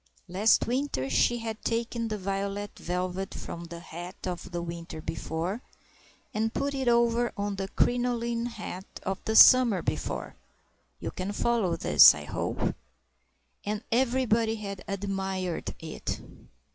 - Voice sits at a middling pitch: No, high, 205 Hz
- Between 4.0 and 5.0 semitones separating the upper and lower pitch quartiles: Yes, average, 4.3 semitones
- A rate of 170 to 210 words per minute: No, slow, 135 wpm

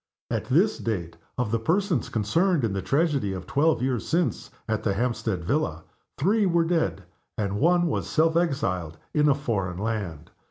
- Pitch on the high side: No, low, 125 Hz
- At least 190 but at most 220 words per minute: No, average, 170 wpm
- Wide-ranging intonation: Yes, wide, 8.5 semitones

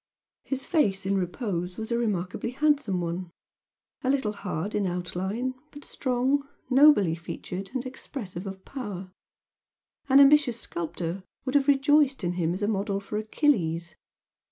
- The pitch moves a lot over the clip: Yes, wide, 6.7 semitones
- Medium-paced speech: Yes, average, 145 wpm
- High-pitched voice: Yes, high, 205 Hz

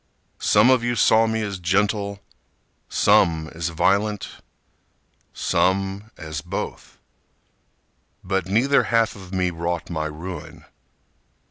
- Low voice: Yes, very low, 95 Hz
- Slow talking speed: Yes, slow, 110 wpm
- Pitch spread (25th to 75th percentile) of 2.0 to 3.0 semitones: No, average, 3.9 semitones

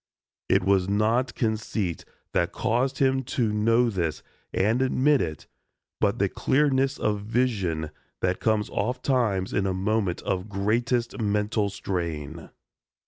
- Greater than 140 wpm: No, slow, 135 wpm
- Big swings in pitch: No, average, 4.2 semitones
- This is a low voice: Yes, low, 105 Hz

